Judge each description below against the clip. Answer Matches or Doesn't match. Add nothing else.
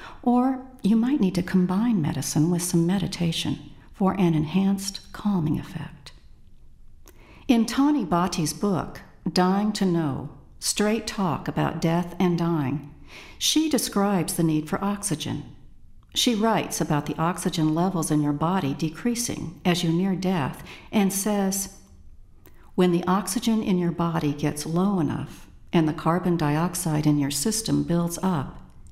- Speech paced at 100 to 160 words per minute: Matches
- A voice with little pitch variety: Doesn't match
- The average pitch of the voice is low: Doesn't match